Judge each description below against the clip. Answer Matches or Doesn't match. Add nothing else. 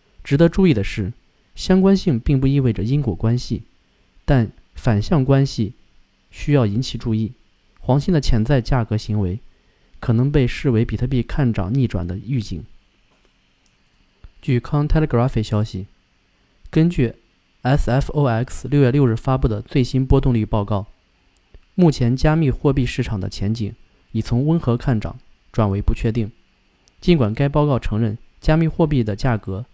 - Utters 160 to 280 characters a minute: Matches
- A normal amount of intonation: Matches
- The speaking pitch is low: Matches